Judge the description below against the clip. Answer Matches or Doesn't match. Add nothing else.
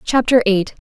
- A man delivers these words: Doesn't match